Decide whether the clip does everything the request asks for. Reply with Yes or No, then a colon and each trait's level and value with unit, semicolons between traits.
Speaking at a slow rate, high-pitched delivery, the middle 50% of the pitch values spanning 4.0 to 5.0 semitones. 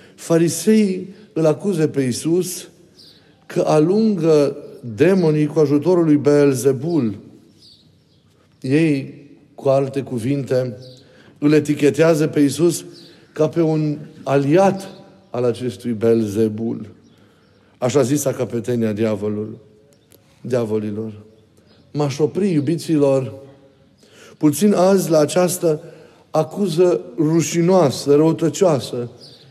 No: slow, 85 wpm; medium, 150 Hz; average, 4.4 semitones